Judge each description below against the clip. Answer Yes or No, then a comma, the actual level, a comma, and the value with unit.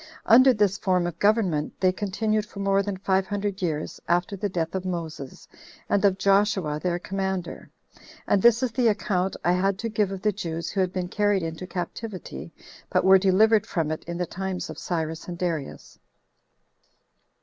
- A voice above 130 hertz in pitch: Yes, high, 190 Hz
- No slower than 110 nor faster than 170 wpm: No, average, 180 wpm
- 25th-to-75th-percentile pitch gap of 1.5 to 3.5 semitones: Yes, average, 2.8 semitones